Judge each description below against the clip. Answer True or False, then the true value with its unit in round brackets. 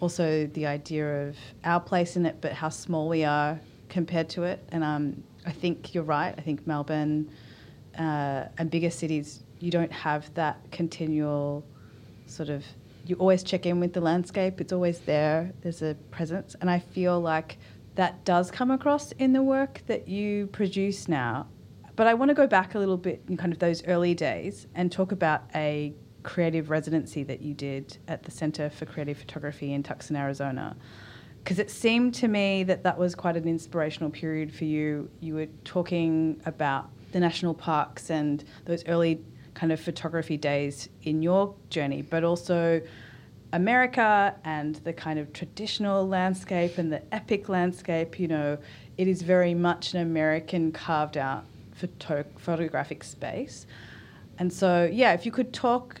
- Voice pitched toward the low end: False (160 Hz)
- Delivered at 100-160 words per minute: False (175 wpm)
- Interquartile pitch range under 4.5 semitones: True (3.3 semitones)